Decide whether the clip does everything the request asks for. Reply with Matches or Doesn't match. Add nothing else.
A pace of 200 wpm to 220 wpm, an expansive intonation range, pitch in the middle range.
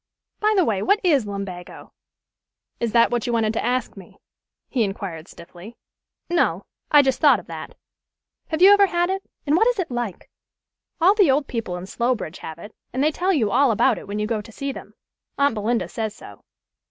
Doesn't match